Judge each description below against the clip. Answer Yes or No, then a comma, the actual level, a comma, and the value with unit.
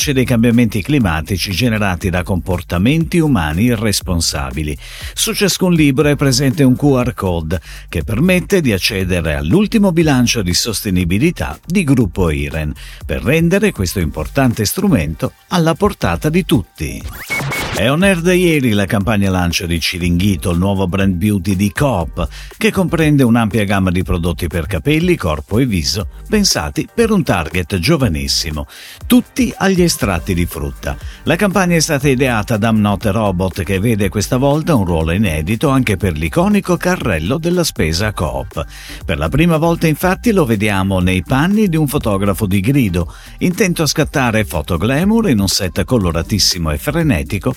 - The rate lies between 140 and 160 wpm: Yes, average, 150 wpm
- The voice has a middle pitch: No, low, 110 Hz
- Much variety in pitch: Yes, wide, 9.0 semitones